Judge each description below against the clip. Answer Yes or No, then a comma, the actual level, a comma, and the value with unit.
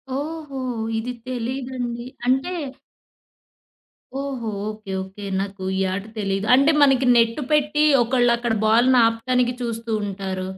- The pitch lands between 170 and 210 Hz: No, high, 240 Hz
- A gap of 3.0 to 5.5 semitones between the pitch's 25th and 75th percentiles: Yes, average, 3.4 semitones